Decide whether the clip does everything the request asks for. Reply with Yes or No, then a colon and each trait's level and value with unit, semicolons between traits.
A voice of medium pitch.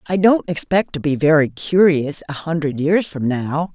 Yes: medium, 160 Hz